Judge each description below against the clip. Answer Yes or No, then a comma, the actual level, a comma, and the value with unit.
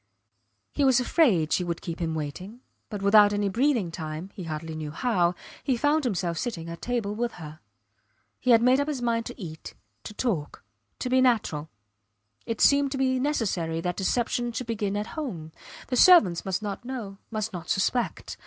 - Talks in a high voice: Yes, high, 210 Hz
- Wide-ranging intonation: Yes, wide, 6.4 semitones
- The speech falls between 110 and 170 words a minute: No, average, 185 wpm